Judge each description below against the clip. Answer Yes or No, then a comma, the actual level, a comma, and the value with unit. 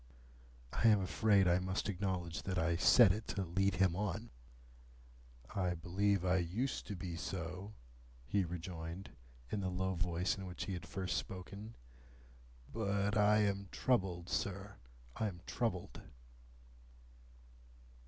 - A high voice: No, very low, 95 Hz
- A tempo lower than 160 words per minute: Yes, slow, 135 wpm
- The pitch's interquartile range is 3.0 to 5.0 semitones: No, narrow, 2.4 semitones